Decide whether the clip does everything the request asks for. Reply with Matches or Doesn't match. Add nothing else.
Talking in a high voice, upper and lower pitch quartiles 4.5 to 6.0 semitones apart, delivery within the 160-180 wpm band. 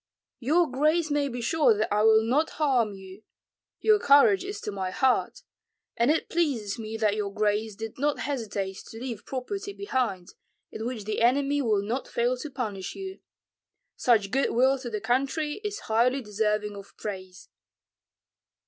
Matches